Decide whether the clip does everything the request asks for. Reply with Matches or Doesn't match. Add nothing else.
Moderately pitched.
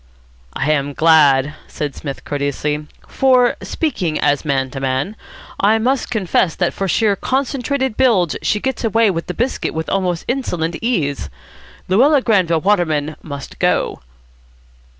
Matches